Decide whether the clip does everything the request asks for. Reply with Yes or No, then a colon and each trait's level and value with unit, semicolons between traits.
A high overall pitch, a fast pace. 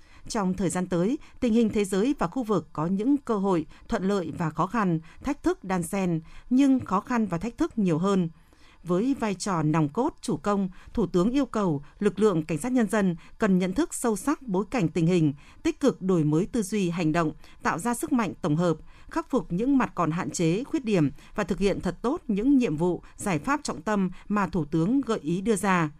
No: high, 200 Hz; average, 230 wpm